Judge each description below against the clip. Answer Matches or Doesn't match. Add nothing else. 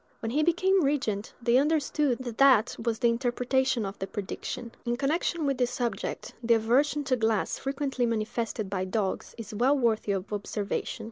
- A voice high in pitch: Matches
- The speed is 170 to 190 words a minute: Matches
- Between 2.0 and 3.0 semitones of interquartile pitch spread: Doesn't match